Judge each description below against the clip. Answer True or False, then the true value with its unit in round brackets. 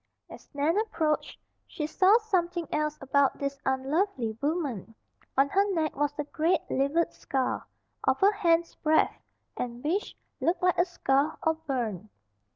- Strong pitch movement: False (4.1 semitones)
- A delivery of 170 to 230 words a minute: False (150 wpm)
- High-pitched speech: True (305 Hz)